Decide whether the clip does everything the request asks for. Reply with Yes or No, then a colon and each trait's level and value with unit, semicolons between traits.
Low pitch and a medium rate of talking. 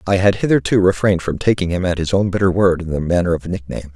No: very low, 90 Hz; fast, 275 wpm